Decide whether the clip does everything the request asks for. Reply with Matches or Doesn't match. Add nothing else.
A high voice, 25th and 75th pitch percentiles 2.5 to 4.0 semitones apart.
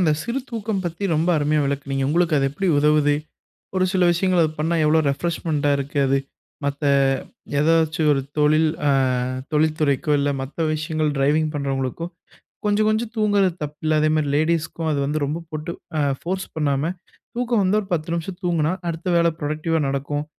Doesn't match